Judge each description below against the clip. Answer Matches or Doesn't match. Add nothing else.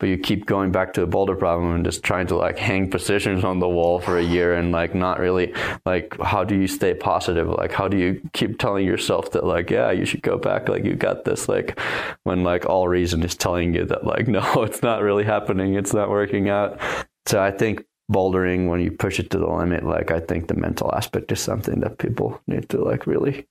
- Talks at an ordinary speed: Doesn't match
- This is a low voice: Matches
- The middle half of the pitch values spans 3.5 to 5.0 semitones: Doesn't match